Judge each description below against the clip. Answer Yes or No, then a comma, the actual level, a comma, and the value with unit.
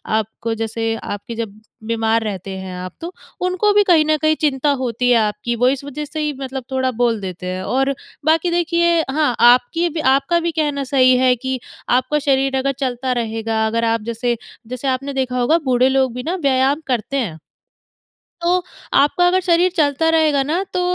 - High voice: Yes, very high, 265 Hz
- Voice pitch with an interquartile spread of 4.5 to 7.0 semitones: Yes, average, 5.0 semitones